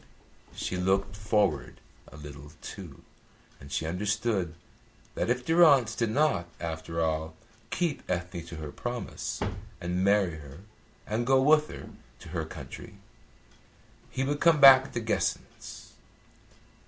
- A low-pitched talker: Yes, low, 100 Hz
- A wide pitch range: Yes, wide, 7.4 semitones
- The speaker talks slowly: Yes, slow, 130 wpm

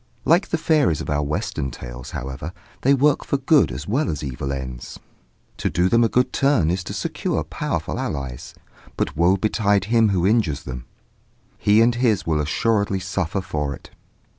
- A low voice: Yes, very low, 95 Hz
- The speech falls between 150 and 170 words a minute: No, average, 185 wpm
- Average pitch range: No, wide, 8.3 semitones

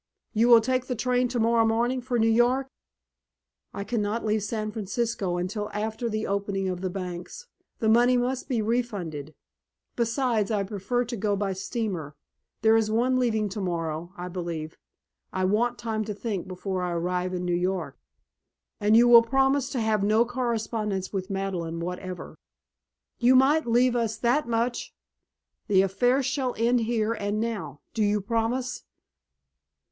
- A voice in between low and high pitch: No, high, 220 Hz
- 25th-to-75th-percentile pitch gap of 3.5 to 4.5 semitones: Yes, average, 3.9 semitones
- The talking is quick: No, average, 160 wpm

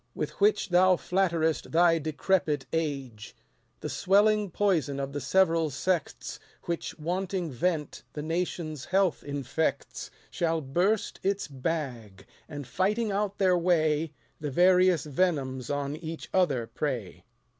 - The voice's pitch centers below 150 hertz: No, medium, 165 Hz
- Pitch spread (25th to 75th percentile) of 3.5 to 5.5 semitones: Yes, average, 4.5 semitones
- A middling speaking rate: No, slow, 125 wpm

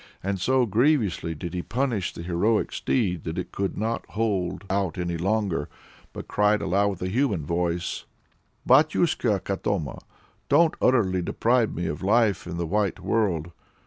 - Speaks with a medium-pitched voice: No, low, 100 Hz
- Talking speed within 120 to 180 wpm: Yes, average, 155 wpm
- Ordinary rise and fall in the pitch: Yes, average, 4.4 semitones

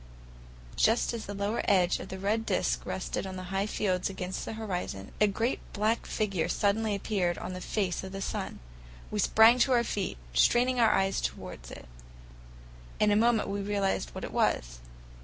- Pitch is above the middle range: Yes, high, 200 Hz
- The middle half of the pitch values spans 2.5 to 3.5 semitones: Yes, average, 2.9 semitones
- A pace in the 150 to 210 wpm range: Yes, average, 185 wpm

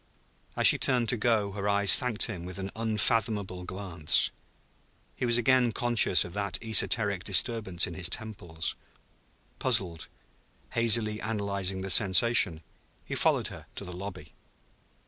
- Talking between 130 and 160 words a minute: Yes, average, 140 wpm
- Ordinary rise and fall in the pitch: Yes, average, 3.6 semitones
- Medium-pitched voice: No, low, 100 Hz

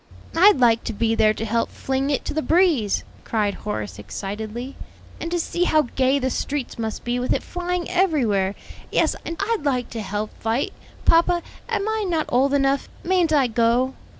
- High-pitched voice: Yes, very high, 260 Hz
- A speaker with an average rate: Yes, average, 185 wpm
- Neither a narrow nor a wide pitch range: No, wide, 6.7 semitones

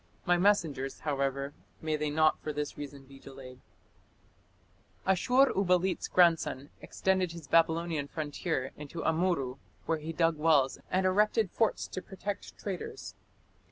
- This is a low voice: No, medium, 160 Hz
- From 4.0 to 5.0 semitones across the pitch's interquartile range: Yes, average, 4.5 semitones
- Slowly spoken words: Yes, slow, 130 wpm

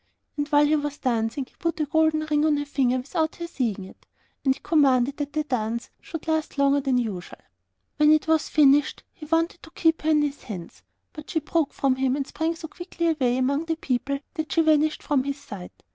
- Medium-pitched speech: No, very high, 290 Hz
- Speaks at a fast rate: Yes, fast, 220 wpm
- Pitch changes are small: No, average, 3.2 semitones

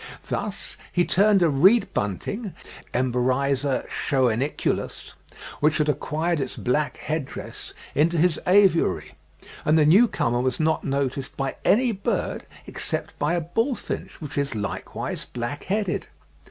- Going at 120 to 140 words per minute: Yes, slow, 135 wpm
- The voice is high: No, medium, 150 Hz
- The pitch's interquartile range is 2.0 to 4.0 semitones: No, average, 5.0 semitones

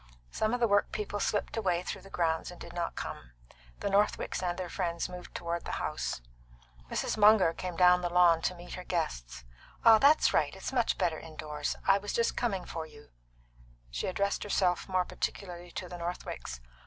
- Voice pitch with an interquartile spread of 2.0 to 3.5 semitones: Yes, average, 2.9 semitones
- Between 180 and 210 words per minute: Yes, average, 190 wpm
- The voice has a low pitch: No, medium, 180 Hz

